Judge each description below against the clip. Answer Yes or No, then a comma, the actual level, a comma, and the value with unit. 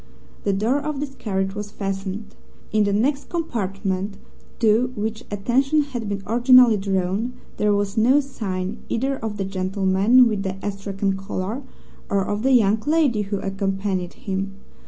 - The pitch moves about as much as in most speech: Yes, average, 3.8 semitones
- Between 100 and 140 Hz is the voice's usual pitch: No, high, 205 Hz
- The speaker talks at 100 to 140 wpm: No, average, 155 wpm